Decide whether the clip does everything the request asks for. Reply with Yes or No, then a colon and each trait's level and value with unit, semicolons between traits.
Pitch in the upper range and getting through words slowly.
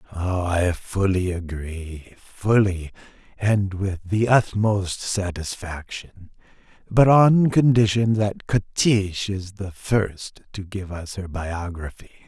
No: low, 100 Hz; slow, 110 wpm